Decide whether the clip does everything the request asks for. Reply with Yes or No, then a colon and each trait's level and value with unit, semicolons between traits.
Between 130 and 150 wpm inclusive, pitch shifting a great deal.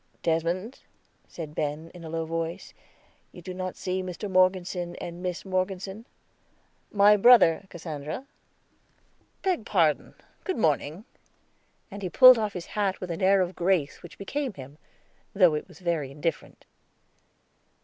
No: average, 140 wpm; average, 3.1 semitones